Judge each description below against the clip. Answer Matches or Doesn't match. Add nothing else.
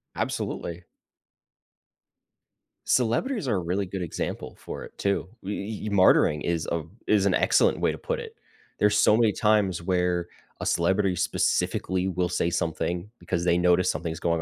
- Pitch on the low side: Matches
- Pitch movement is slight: Doesn't match